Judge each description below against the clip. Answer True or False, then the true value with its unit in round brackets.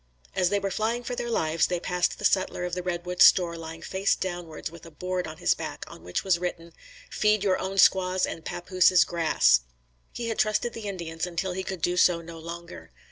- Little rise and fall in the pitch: True (2.2 semitones)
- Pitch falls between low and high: True (180 Hz)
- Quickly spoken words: True (215 wpm)